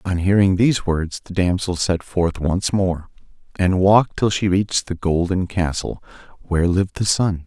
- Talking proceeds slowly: No, average, 175 wpm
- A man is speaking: Yes, male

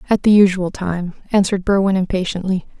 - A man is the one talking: No, female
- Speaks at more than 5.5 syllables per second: Yes, 6.0 syllables/s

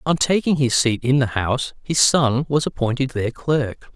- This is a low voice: Yes, low, 130 Hz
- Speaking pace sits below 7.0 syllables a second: Yes, 4.6 syllables/s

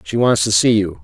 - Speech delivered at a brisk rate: Yes, fast, 290 wpm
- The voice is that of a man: Yes, male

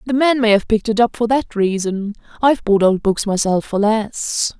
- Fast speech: Yes, fast, 210 wpm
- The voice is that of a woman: Yes, female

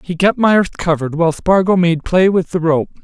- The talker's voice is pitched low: No, medium, 175 Hz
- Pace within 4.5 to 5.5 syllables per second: Yes, 5.3 syllables/s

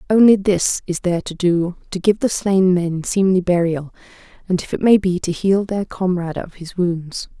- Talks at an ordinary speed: Yes, average, 195 wpm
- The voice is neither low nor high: Yes, medium, 180 Hz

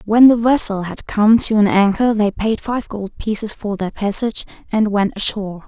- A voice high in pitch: Yes, high, 215 Hz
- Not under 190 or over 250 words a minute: Yes, average, 200 wpm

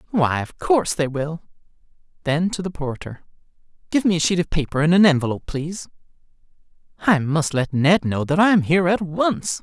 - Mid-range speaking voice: Yes, medium, 165 Hz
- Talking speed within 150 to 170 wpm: No, average, 180 wpm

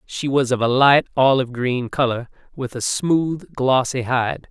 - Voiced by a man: Yes, male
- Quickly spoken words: No, average, 175 wpm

